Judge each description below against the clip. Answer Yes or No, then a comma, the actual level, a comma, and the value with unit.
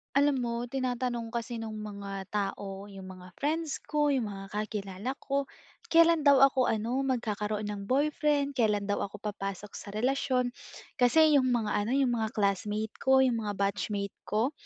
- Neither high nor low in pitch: No, high, 230 Hz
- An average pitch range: Yes, average, 4.5 semitones